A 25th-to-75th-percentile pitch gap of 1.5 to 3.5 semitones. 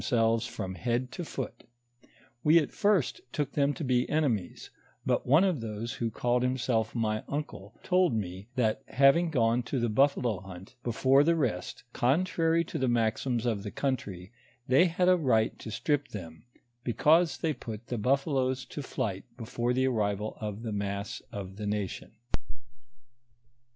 No: average, 4.7 semitones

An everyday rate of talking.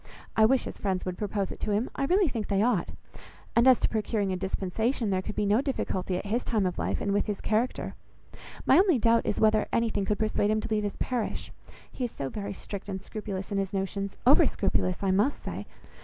No: fast, 230 wpm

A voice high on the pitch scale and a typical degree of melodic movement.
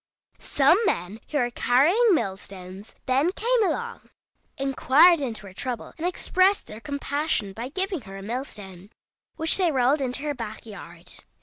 No: very high, 265 Hz; wide, 7.3 semitones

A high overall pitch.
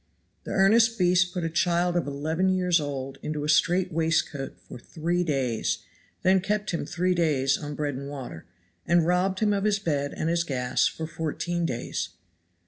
No: medium, 165 Hz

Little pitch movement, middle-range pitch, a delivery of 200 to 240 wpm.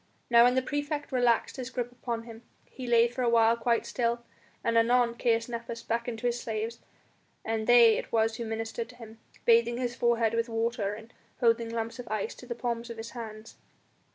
No: narrow, 1.1 semitones; high, 235 Hz; fast, 205 wpm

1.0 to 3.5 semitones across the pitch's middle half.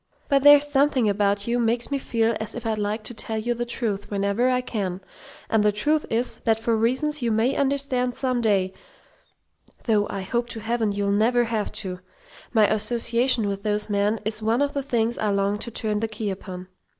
Yes: average, 2.8 semitones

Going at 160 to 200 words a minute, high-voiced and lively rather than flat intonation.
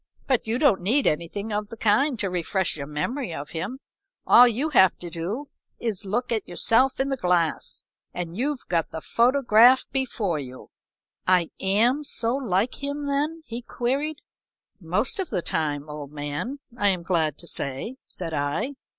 Yes: average, 175 wpm; high, 210 Hz; wide, 7.4 semitones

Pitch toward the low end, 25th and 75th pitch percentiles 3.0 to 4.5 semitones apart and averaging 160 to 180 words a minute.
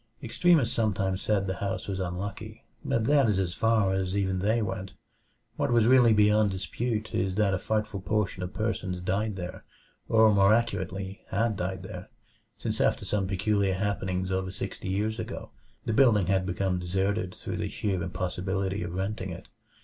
No: low, 100 Hz; narrow, 2.5 semitones; average, 170 wpm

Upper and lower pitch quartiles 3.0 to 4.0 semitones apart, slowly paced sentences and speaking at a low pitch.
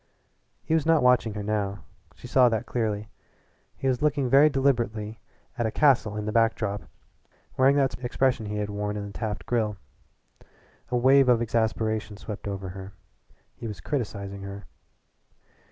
No: average, 3.4 semitones; average, 165 wpm; low, 110 Hz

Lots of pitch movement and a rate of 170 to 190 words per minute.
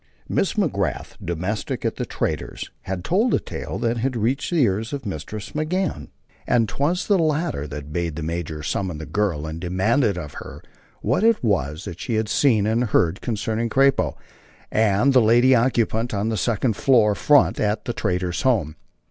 Yes: wide, 6.2 semitones; average, 175 wpm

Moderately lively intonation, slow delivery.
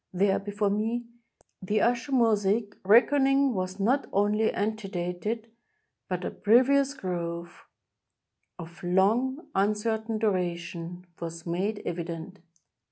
Yes: average, 4.2 semitones; slow, 105 wpm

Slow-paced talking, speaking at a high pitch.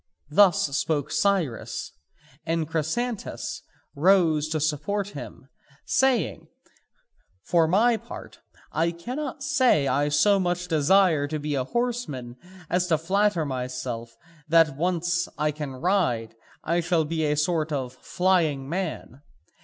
No: slow, 120 wpm; medium, 165 Hz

